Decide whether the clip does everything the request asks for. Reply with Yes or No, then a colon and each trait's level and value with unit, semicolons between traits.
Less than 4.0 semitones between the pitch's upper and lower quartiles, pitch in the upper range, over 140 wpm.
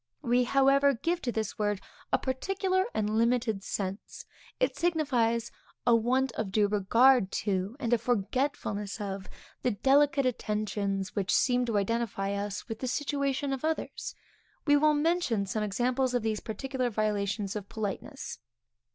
No: average, 4.5 semitones; high, 235 Hz; average, 150 wpm